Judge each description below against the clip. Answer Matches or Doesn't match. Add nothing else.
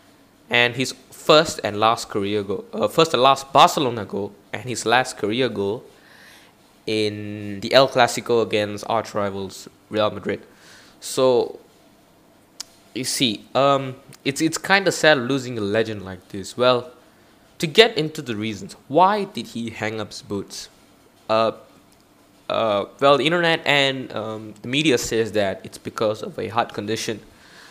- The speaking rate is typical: Matches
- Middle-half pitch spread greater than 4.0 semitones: Matches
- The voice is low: Matches